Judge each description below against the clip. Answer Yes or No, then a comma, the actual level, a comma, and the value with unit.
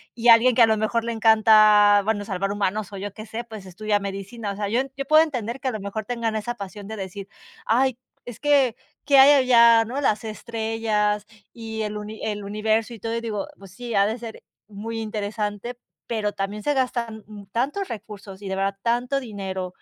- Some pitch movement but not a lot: No, narrow, 2.3 semitones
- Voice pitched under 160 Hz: No, high, 220 Hz